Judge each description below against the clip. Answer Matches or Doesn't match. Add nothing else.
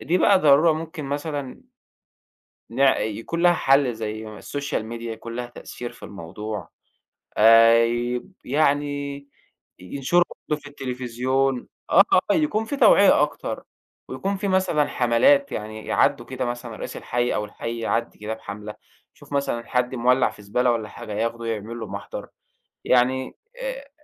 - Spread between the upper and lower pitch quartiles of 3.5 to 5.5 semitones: Matches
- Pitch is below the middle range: Matches